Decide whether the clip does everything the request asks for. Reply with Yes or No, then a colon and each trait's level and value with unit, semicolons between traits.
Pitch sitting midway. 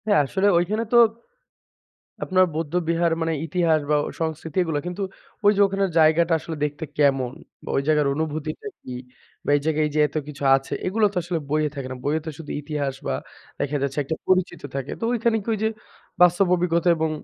Yes: medium, 160 Hz